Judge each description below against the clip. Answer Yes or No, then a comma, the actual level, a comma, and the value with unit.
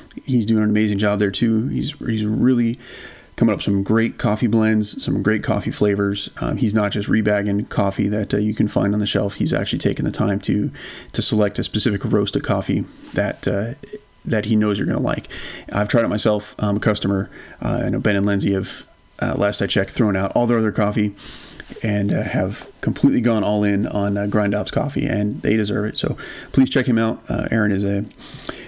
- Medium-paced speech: No, fast, 220 wpm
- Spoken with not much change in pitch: Yes, narrow, 1.8 semitones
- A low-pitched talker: Yes, low, 105 Hz